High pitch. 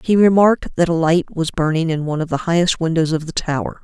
No: medium, 165 Hz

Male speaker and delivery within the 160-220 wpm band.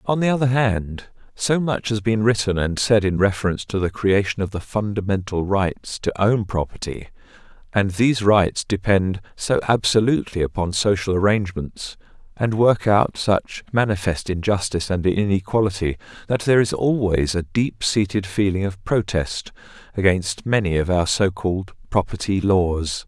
No: male; average, 150 wpm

